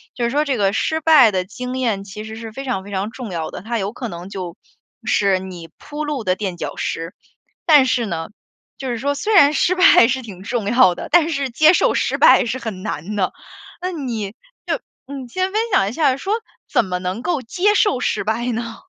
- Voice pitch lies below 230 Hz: No, high, 235 Hz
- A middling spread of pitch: No, wide, 6.1 semitones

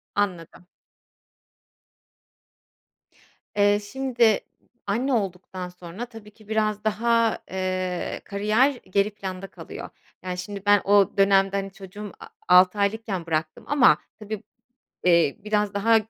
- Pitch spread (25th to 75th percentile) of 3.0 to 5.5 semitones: No, narrow, 2.6 semitones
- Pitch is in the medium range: No, high, 205 Hz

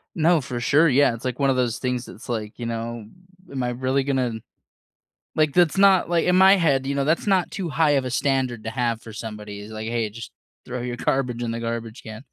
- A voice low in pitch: Yes, low, 125 Hz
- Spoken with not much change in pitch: No, average, 3.8 semitones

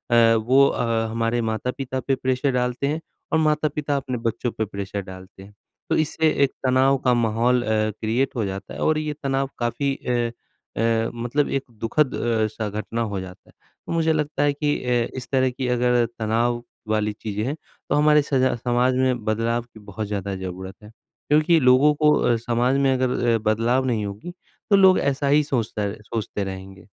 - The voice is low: Yes, low, 120 Hz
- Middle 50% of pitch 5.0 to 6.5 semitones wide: No, average, 3.9 semitones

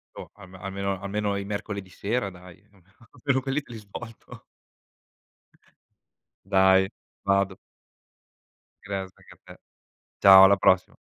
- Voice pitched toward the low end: Yes, low, 100 Hz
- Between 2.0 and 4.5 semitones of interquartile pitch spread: No, narrow, 1.5 semitones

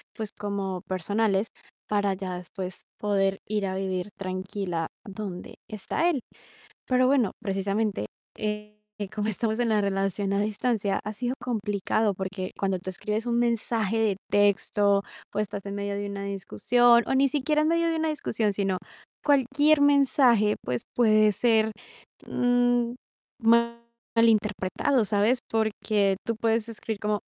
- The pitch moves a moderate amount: Yes, average, 3.2 semitones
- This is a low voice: No, high, 210 Hz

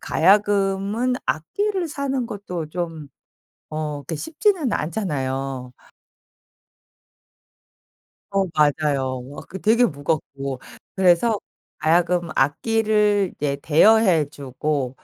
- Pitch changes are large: Yes, wide, 6.5 semitones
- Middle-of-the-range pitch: Yes, medium, 175 Hz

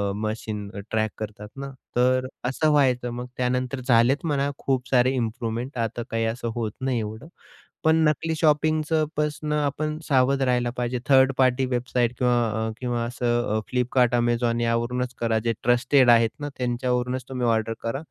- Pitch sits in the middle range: No, low, 125 Hz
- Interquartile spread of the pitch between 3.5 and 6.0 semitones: No, narrow, 2.4 semitones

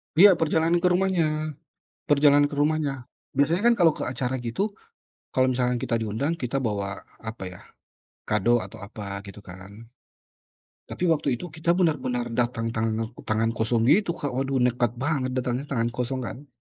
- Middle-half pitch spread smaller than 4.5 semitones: No, average, 5.1 semitones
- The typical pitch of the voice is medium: No, low, 130 Hz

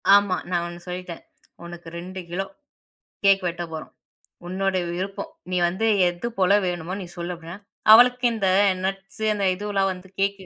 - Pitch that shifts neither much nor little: No, narrow, 2.1 semitones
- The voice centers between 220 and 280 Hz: No, medium, 185 Hz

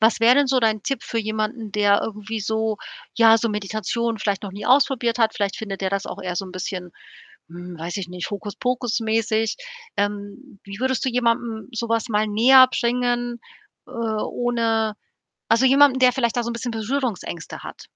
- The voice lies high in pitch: Yes, high, 225 Hz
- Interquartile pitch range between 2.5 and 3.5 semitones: Yes, average, 2.8 semitones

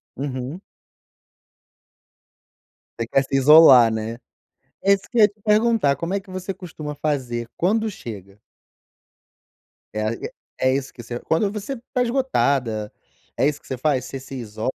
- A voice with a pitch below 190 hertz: Yes, medium, 140 Hz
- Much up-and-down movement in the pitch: Yes, wide, 8.2 semitones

